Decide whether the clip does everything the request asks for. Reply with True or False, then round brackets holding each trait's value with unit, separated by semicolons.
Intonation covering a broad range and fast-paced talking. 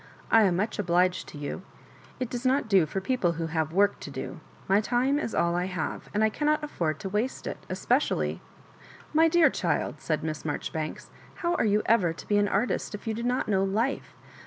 True (6.1 semitones; 225 wpm)